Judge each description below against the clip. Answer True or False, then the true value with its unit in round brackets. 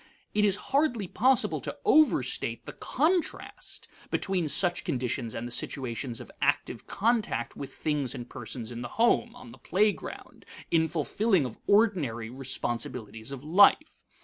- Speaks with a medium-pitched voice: True (155 Hz)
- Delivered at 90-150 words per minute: True (145 wpm)